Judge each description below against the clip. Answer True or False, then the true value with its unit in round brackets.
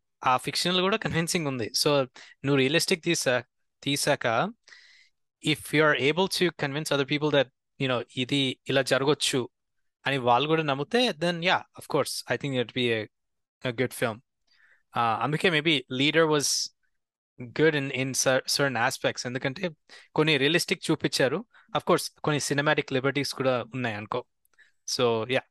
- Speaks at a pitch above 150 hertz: False (140 Hz)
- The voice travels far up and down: False (3.8 semitones)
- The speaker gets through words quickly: True (140 wpm)